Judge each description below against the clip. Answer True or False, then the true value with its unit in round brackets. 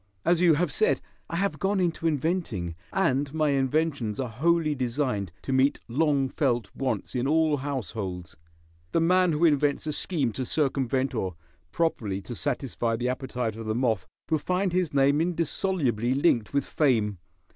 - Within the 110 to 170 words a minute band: True (165 wpm)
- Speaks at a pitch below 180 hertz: True (140 Hz)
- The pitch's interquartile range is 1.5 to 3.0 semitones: False (5.1 semitones)